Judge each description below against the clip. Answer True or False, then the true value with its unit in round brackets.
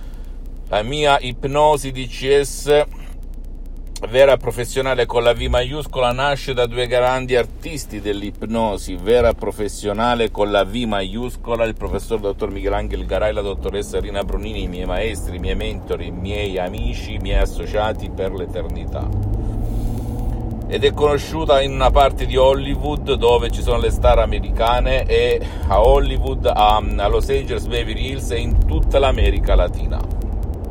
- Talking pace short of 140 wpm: False (145 wpm)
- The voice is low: True (105 Hz)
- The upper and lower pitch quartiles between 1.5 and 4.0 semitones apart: False (4.6 semitones)